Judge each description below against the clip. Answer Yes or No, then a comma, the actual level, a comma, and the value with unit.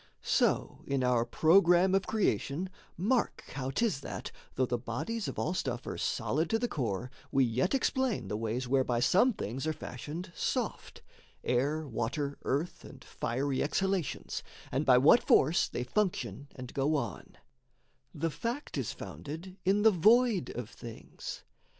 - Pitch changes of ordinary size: No, wide, 7.2 semitones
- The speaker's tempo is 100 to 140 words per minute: No, average, 155 wpm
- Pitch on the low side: No, medium, 145 Hz